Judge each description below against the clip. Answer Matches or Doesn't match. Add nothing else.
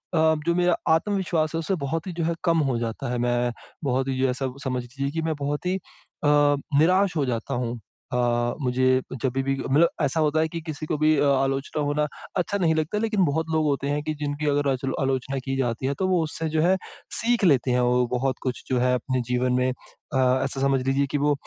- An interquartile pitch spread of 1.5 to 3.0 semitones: Doesn't match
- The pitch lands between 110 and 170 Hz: Matches